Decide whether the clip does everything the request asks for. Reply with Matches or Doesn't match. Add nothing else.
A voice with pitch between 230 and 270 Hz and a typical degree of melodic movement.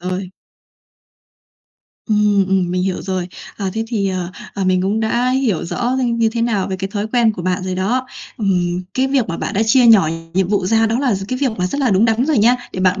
Doesn't match